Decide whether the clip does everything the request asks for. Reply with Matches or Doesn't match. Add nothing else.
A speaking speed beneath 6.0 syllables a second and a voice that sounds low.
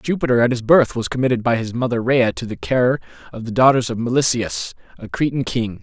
Matches